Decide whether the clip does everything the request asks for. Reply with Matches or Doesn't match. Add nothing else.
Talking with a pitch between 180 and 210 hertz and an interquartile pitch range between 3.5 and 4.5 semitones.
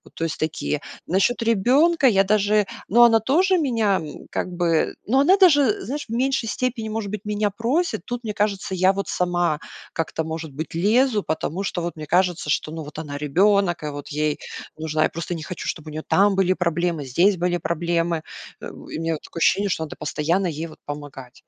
Doesn't match